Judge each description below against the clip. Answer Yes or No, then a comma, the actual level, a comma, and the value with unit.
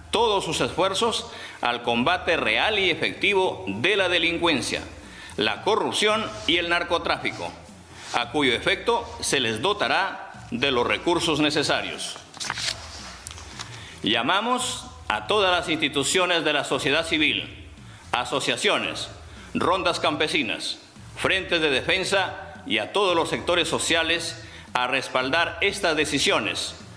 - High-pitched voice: No, medium, 165 Hz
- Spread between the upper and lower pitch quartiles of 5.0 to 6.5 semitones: Yes, wide, 5.6 semitones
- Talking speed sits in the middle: No, slow, 115 wpm